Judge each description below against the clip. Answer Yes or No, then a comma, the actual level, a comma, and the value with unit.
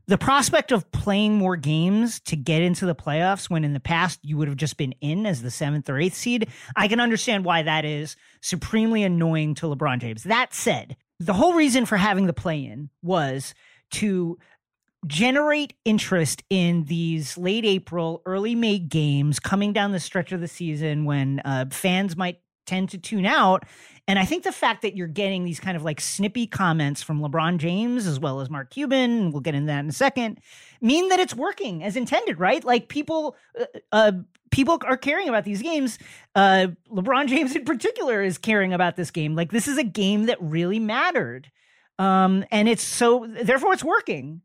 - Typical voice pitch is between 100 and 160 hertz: No, high, 190 Hz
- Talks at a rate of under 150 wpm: No, average, 195 wpm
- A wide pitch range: Yes, wide, 6.2 semitones